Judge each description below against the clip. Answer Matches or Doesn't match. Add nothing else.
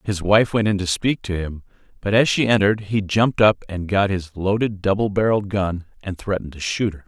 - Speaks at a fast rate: Matches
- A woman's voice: Doesn't match